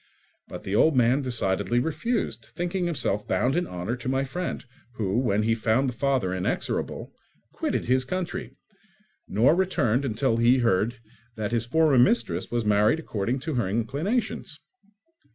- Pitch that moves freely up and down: No, average, 4.5 semitones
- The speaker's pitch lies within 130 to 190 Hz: No, low, 120 Hz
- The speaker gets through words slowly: No, average, 155 wpm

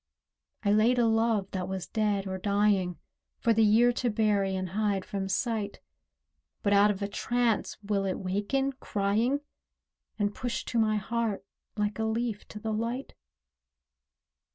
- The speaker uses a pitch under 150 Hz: No, high, 210 Hz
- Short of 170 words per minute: Yes, average, 155 wpm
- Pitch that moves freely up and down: No, narrow, 2.5 semitones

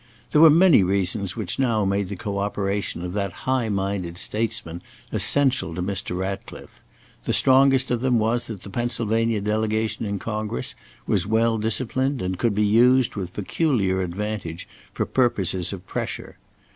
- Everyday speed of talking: Yes, average, 160 wpm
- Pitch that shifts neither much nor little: Yes, average, 3.7 semitones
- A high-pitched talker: No, low, 105 Hz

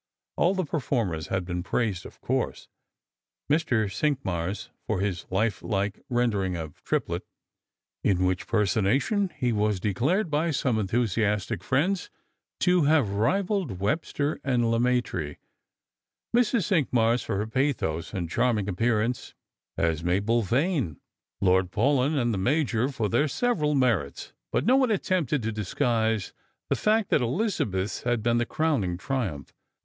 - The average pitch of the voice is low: Yes, low, 115 Hz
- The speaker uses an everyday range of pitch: No, wide, 6.9 semitones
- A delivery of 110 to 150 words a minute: Yes, average, 145 wpm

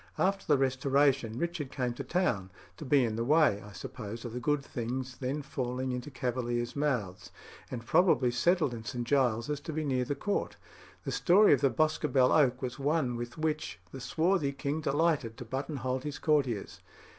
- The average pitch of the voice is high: No, low, 130 Hz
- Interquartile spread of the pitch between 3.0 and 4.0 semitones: Yes, average, 3.6 semitones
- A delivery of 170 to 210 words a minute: Yes, average, 180 wpm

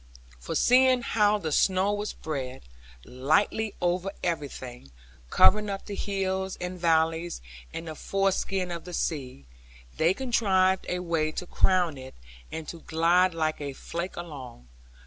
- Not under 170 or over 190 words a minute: No, average, 145 wpm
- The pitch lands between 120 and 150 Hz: No, medium, 175 Hz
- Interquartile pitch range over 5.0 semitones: No, average, 3.7 semitones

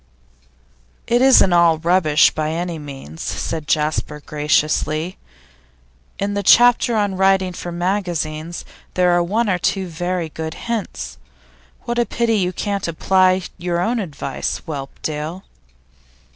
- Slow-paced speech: Yes, slow, 130 wpm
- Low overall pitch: No, medium, 175 Hz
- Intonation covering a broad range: No, average, 3.8 semitones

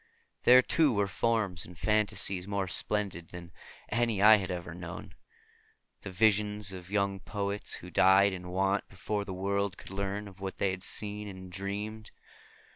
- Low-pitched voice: Yes, low, 100 Hz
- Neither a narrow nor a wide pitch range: No, narrow, 2.0 semitones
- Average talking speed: Yes, average, 165 wpm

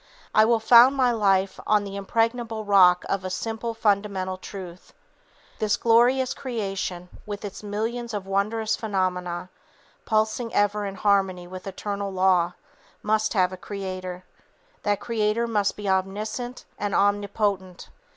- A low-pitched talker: No, high, 205 Hz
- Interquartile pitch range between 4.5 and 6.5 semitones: No, average, 2.8 semitones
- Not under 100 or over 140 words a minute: Yes, slow, 135 wpm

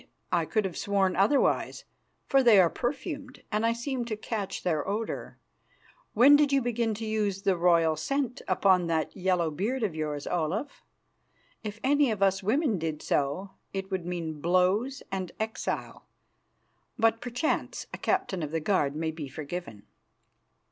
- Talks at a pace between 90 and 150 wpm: No, average, 160 wpm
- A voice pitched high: Yes, high, 195 Hz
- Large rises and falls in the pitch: Yes, wide, 5.7 semitones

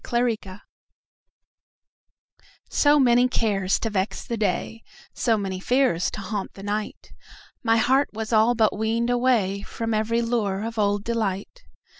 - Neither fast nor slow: No, slow, 130 wpm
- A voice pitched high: Yes, high, 220 Hz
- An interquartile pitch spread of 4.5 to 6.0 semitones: No, average, 2.8 semitones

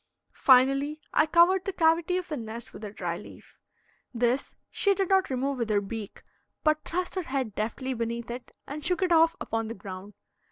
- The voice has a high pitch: Yes, very high, 265 Hz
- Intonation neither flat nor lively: No, wide, 6.8 semitones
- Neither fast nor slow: Yes, average, 195 wpm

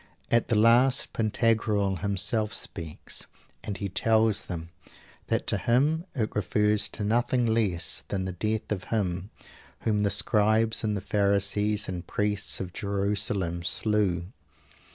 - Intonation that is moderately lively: No, narrow, 2.2 semitones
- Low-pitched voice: Yes, low, 105 Hz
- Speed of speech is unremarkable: No, slow, 130 wpm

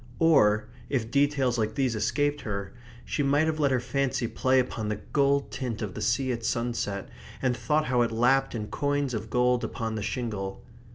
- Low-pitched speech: Yes, low, 125 Hz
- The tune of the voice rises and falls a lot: No, average, 3.8 semitones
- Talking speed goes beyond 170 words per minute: Yes, average, 190 wpm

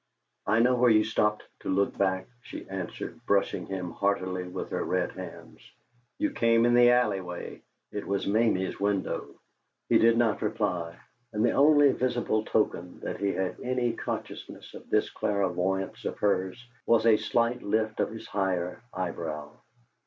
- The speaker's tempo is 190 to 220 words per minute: No, average, 160 wpm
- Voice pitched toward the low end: Yes, low, 105 Hz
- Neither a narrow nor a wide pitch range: Yes, average, 3.8 semitones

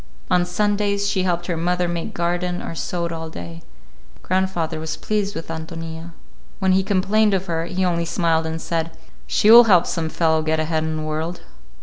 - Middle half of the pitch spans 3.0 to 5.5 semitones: No, narrow, 2.6 semitones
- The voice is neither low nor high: Yes, medium, 170 Hz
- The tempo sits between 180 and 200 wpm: Yes, average, 190 wpm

